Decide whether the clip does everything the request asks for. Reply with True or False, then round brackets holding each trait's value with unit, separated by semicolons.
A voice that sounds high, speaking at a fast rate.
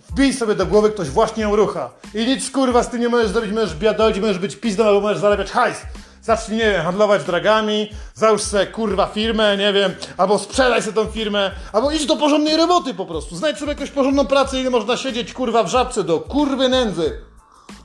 True (220 Hz; 210 wpm)